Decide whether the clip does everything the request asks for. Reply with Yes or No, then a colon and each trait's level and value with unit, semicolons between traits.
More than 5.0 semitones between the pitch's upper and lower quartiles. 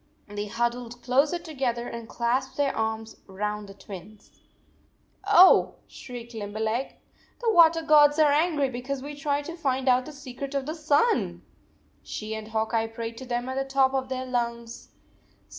No: average, 4.1 semitones